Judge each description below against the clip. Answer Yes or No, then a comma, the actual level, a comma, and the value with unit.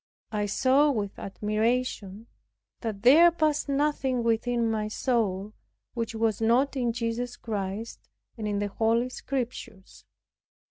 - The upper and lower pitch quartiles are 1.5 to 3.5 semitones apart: Yes, average, 3.0 semitones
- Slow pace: Yes, slow, 125 wpm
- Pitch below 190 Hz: No, high, 230 Hz